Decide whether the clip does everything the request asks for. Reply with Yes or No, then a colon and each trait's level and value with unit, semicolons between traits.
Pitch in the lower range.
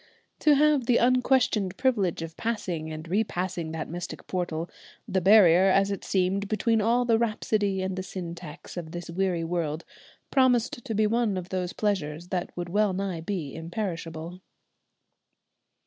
No: medium, 185 Hz